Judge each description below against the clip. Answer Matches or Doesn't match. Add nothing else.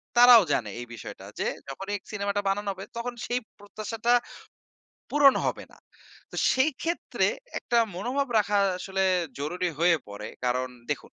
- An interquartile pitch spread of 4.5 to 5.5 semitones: Matches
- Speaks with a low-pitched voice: Doesn't match